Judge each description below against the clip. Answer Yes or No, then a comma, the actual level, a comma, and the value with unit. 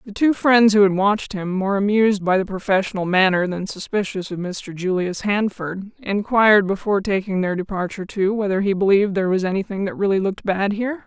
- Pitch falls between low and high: No, high, 195 Hz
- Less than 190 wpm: No, average, 195 wpm